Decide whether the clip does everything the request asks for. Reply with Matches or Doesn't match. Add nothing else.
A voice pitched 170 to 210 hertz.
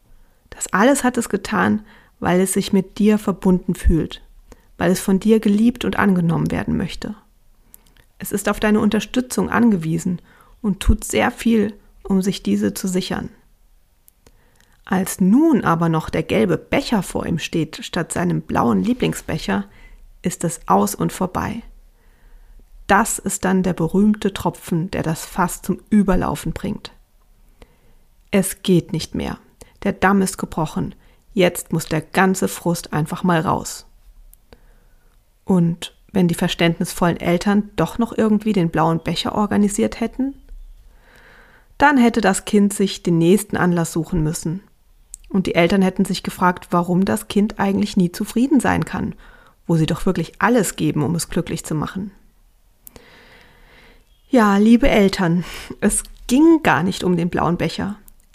Matches